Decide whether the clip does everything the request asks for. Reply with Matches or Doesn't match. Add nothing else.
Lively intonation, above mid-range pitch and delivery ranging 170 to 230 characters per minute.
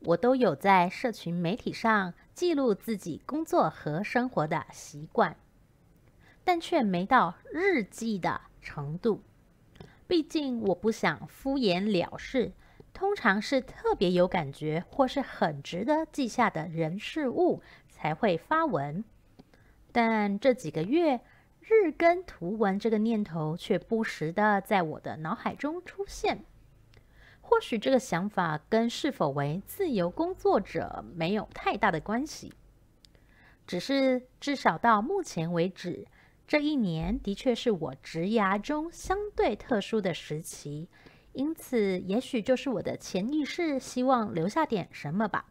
Matches